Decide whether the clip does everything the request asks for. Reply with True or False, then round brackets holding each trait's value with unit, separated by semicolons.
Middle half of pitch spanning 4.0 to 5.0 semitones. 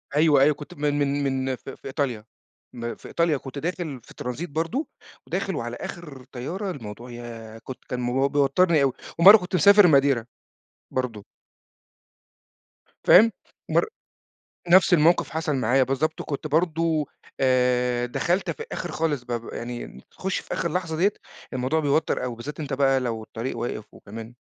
True (4.7 semitones)